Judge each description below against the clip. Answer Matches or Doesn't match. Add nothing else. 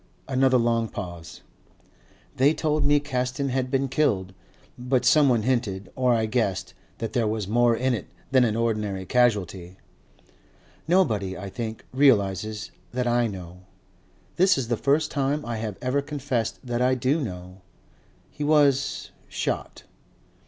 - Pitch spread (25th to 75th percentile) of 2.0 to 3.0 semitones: Doesn't match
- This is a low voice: Matches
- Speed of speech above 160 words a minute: Doesn't match